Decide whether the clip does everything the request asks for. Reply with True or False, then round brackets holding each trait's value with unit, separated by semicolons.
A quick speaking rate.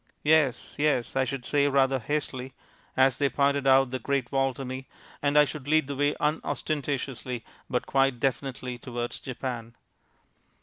False (160 wpm)